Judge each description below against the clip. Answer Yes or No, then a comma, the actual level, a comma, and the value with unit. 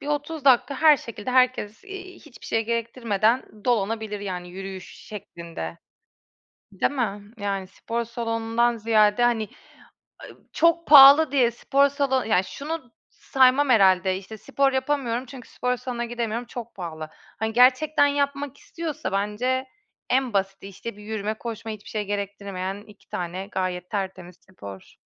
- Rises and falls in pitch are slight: No, average, 4.7 semitones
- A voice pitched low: No, high, 230 Hz